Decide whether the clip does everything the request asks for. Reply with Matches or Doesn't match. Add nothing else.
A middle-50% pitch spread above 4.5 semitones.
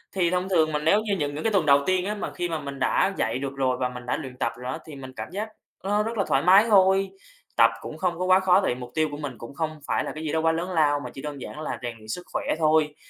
Matches